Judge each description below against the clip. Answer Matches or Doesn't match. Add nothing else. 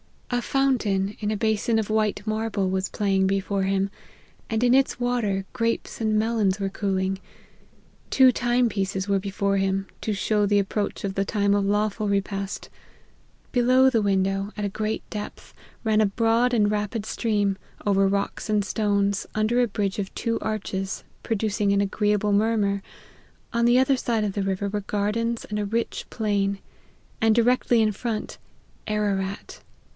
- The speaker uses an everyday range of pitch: Doesn't match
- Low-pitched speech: Doesn't match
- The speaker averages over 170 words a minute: Doesn't match